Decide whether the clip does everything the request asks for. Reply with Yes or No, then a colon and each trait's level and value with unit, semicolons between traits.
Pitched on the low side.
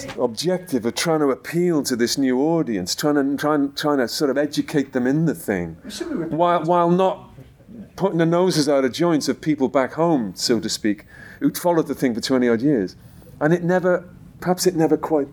No: medium, 150 Hz